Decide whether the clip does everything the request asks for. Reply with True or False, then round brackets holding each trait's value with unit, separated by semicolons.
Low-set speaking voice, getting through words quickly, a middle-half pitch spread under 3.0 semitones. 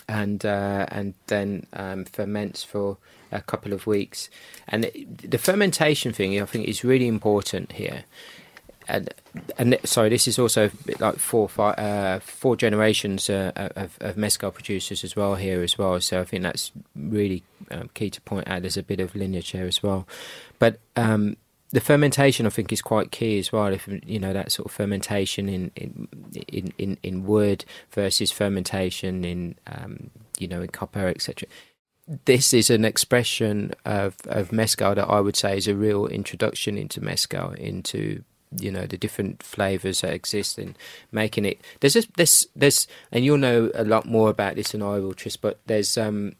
False (105 Hz; 185 wpm; 2.4 semitones)